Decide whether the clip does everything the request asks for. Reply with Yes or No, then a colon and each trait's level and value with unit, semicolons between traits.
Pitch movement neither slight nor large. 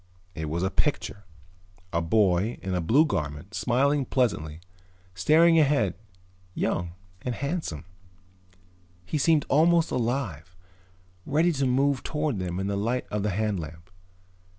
No: wide, 8.2 semitones